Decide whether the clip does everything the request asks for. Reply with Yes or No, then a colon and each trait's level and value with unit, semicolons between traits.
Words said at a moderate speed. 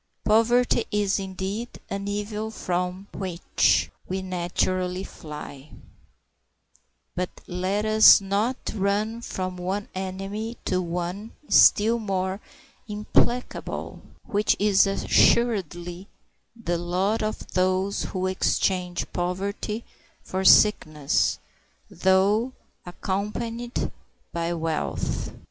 No: slow, 90 wpm